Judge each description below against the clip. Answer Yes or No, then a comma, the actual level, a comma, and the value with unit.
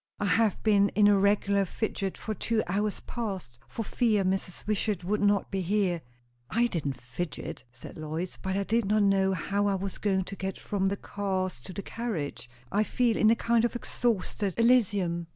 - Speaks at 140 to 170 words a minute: No, average, 190 wpm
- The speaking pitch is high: Yes, high, 200 Hz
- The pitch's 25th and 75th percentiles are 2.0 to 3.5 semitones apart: Yes, narrow, 2.4 semitones